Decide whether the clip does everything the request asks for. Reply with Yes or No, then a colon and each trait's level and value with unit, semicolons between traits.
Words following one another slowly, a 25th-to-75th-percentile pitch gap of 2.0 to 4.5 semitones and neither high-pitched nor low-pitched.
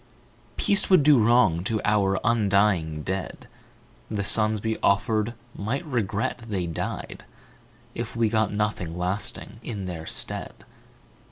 No: slow, 125 wpm; average, 3.0 semitones; low, 105 Hz